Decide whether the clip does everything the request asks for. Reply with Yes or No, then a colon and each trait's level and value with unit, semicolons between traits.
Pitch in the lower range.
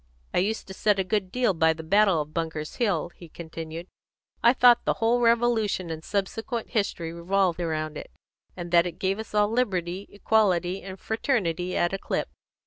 No: high, 190 Hz